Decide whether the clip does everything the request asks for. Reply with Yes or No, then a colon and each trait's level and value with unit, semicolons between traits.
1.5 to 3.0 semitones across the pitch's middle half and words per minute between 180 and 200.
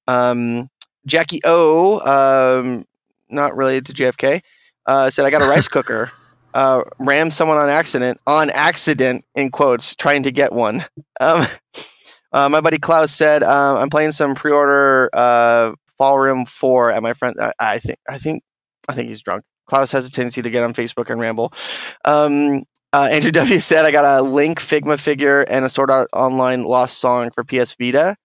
Yes: average, 2.7 semitones; average, 185 wpm